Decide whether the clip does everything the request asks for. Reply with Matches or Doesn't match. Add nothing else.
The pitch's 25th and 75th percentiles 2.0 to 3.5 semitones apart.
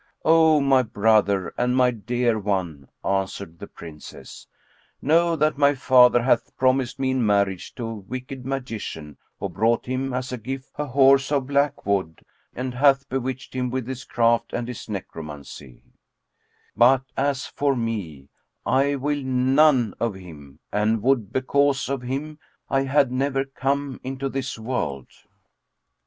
Doesn't match